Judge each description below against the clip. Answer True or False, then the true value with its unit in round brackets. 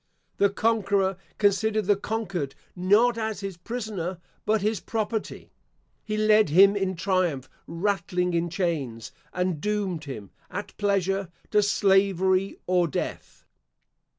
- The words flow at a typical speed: False (125 wpm)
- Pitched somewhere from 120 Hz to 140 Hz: False (195 Hz)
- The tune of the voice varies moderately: True (3.0 semitones)